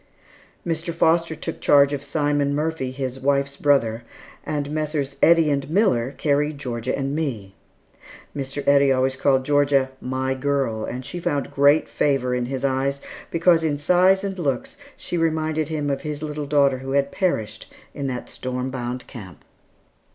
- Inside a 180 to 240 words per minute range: No, average, 160 wpm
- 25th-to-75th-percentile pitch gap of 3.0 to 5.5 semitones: No, narrow, 2.6 semitones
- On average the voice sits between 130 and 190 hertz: Yes, medium, 140 Hz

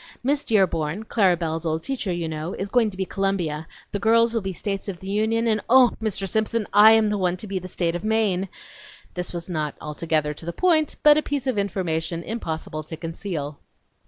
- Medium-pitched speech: No, high, 195 Hz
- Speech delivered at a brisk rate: Yes, fast, 215 wpm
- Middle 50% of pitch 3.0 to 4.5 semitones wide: No, average, 4.9 semitones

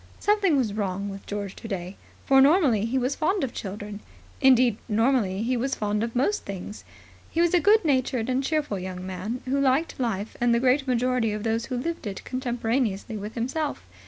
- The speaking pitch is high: Yes, high, 240 Hz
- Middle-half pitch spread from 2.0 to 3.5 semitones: No, average, 4.5 semitones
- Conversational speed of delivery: Yes, average, 190 wpm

